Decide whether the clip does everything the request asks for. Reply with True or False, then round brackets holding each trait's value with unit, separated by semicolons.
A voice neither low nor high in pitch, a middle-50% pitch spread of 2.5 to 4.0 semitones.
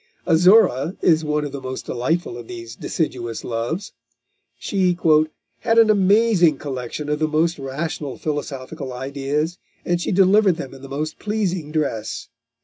False (155 Hz; 4.8 semitones)